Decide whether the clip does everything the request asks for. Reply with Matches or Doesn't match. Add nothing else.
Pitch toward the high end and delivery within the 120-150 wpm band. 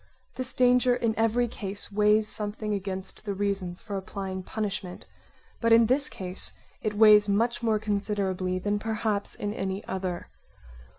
Matches